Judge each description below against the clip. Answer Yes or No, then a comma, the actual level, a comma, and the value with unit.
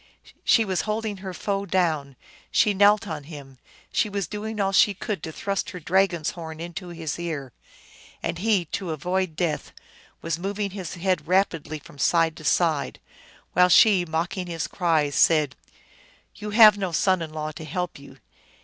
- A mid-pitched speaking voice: Yes, medium, 175 Hz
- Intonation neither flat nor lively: Yes, average, 3.8 semitones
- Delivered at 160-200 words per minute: Yes, average, 180 wpm